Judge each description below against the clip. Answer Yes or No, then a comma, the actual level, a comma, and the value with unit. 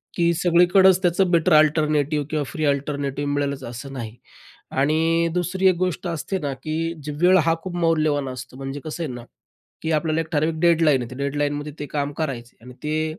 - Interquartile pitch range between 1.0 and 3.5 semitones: Yes, average, 2.9 semitones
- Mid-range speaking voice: Yes, medium, 155 Hz